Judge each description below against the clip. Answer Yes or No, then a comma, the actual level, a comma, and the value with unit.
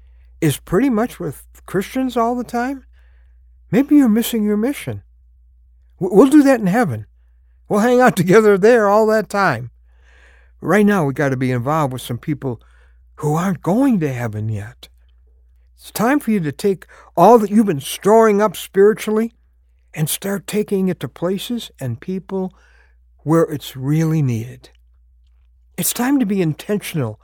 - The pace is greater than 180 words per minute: No, average, 160 wpm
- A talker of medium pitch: Yes, medium, 155 Hz